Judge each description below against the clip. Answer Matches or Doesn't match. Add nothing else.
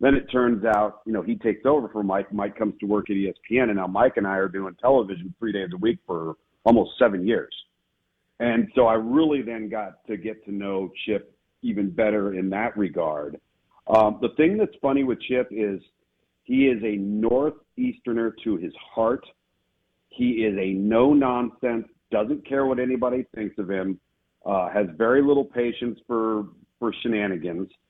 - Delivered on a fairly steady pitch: Doesn't match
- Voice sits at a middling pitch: Doesn't match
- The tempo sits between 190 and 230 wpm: Doesn't match